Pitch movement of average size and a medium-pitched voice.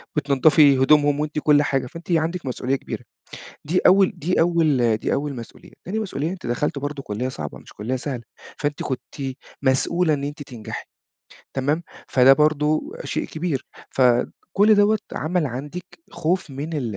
Yes: average, 3.8 semitones; medium, 145 Hz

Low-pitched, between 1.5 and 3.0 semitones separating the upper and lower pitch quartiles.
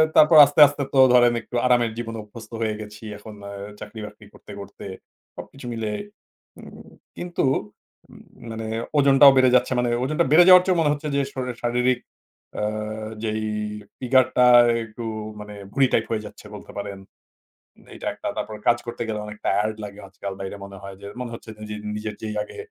No: low, 115 Hz; average, 3.6 semitones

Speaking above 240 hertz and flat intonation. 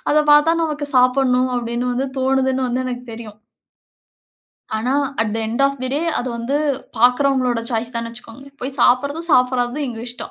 Yes: very high, 250 Hz; narrow, 2.3 semitones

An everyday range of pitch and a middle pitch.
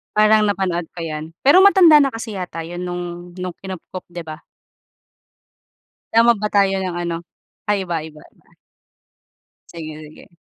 Yes: average, 3.6 semitones; medium, 180 Hz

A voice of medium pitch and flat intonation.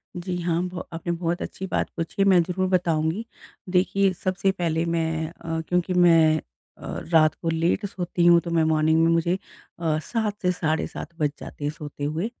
Yes: medium, 170 Hz; narrow, 2.0 semitones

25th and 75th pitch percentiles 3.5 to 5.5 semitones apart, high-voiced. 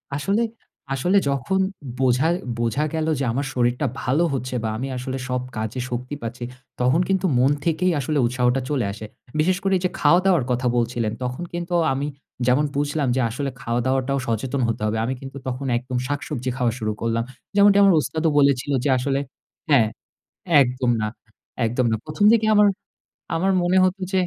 No: average, 4.2 semitones; low, 135 Hz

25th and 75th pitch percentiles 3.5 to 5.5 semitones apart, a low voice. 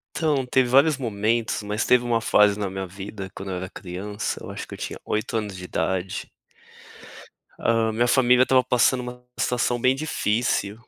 Yes: average, 3.8 semitones; low, 115 Hz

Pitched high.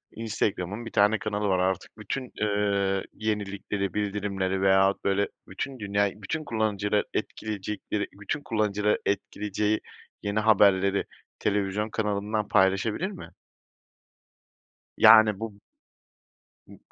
No: low, 105 Hz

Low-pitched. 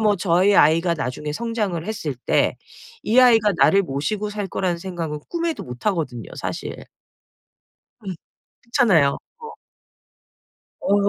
No: high, 190 Hz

